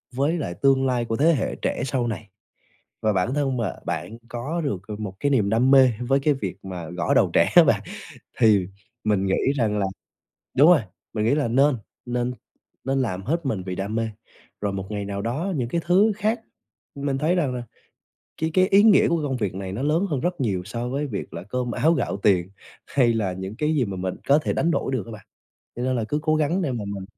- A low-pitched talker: Yes, low, 125 Hz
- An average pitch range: No, wide, 5.9 semitones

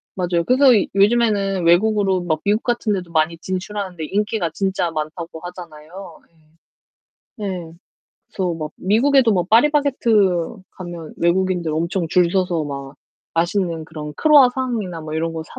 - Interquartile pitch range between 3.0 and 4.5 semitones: Yes, average, 3.9 semitones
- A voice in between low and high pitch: Yes, medium, 180 Hz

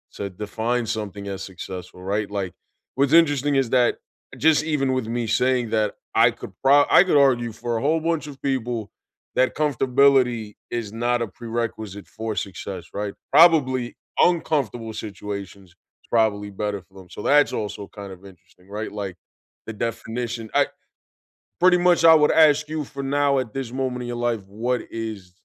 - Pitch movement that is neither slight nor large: Yes, average, 4.8 semitones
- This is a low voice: Yes, low, 115 Hz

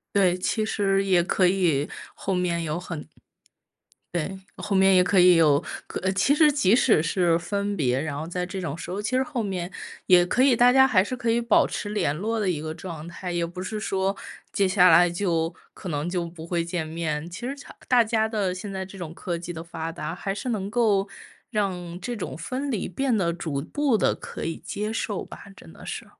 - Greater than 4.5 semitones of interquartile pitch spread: No, average, 3.7 semitones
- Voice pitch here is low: No, medium, 185 Hz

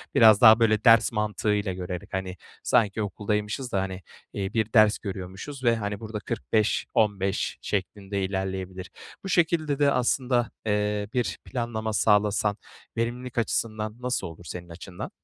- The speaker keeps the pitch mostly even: No, average, 3.1 semitones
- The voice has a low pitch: Yes, low, 105 Hz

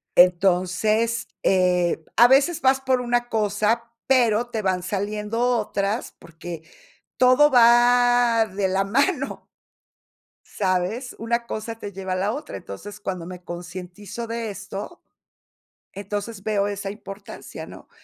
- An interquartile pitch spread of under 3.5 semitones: No, average, 3.9 semitones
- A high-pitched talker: Yes, high, 210 Hz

